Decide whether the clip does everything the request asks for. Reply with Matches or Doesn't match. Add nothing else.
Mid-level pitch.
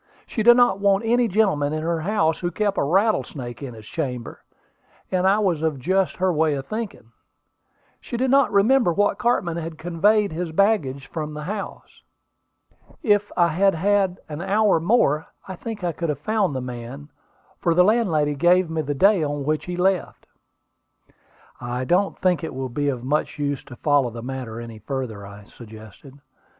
Matches